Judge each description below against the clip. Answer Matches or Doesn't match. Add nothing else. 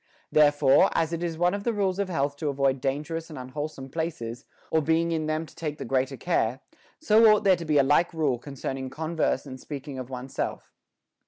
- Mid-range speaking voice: Matches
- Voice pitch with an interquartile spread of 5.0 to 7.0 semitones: Doesn't match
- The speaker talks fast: Matches